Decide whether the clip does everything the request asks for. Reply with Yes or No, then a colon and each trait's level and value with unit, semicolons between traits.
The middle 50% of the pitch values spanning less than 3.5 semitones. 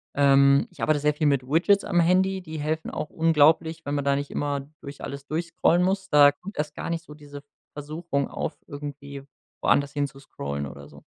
Yes: average, 2.7 semitones